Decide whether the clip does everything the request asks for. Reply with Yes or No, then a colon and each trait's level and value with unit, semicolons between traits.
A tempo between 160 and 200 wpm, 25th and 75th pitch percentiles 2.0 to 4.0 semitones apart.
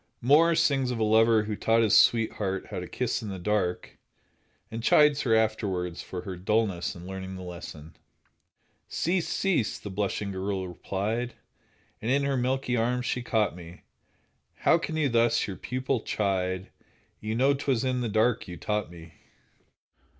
No: average, 165 wpm; average, 4.8 semitones